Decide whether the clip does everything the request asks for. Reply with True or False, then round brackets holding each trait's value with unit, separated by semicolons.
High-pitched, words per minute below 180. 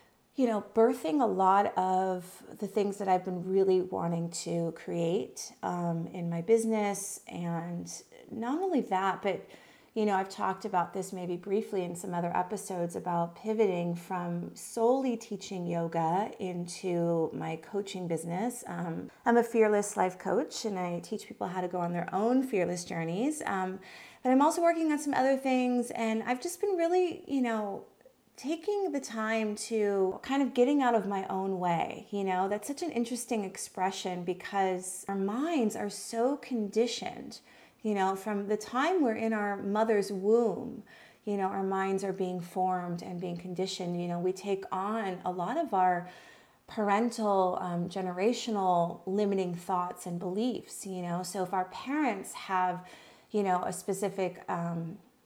True (195 Hz; 165 wpm)